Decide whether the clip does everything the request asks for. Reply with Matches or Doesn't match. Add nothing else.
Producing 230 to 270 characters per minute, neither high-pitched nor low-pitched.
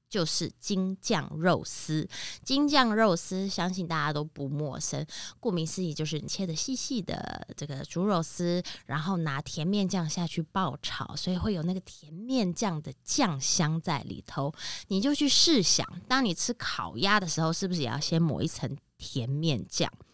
Matches